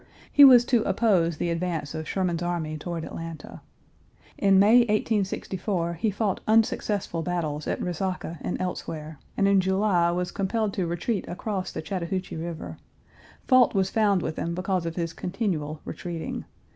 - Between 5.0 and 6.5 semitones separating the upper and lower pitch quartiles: No, average, 3.2 semitones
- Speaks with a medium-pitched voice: Yes, medium, 180 Hz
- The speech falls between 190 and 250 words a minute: No, average, 155 wpm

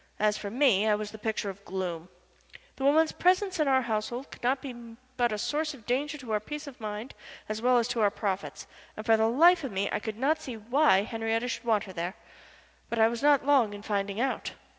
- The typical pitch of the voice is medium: No, high, 230 Hz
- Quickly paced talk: Yes, fast, 235 wpm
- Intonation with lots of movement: No, average, 4.6 semitones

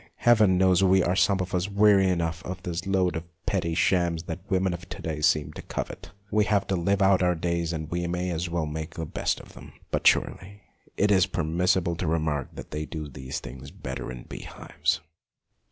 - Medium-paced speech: No, fast, 220 wpm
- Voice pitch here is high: No, very low, 90 Hz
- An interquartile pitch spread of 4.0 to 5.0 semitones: No, average, 2.7 semitones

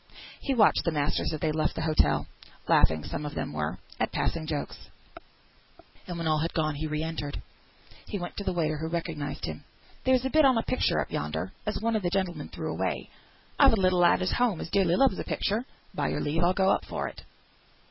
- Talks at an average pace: No, fast, 225 wpm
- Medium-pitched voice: Yes, medium, 170 Hz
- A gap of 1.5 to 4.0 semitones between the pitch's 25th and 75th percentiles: No, average, 4.5 semitones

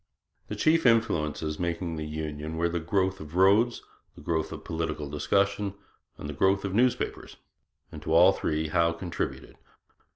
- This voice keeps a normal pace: Yes, average, 160 wpm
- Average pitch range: Yes, average, 4.1 semitones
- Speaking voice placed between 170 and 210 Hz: No, very low, 85 Hz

